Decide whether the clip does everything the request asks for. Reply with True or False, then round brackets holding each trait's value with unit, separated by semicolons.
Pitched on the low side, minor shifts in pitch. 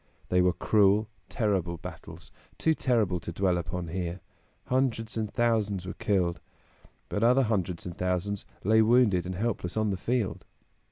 False (100 Hz; 3.9 semitones)